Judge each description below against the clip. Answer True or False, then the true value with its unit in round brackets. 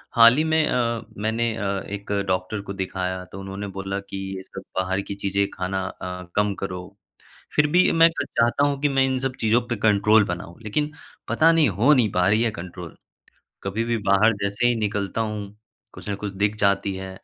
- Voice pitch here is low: True (100 Hz)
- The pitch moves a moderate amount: True (3.3 semitones)